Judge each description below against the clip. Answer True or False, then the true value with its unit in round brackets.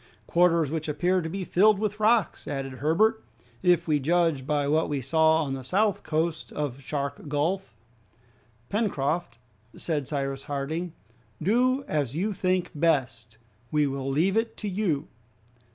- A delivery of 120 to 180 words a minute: True (150 wpm)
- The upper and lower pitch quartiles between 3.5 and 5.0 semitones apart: True (4.7 semitones)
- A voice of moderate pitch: True (160 Hz)